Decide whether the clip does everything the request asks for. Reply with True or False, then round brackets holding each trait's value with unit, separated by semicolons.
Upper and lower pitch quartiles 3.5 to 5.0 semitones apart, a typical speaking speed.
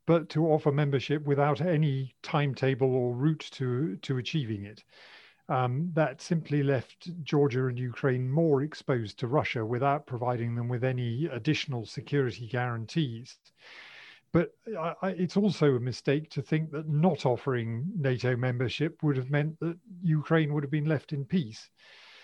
True (3.8 semitones; 155 wpm)